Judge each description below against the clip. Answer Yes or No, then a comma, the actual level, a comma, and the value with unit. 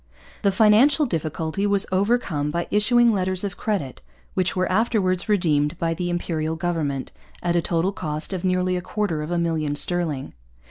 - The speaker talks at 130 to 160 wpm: No, average, 170 wpm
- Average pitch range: Yes, average, 3.9 semitones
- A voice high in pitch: No, medium, 180 Hz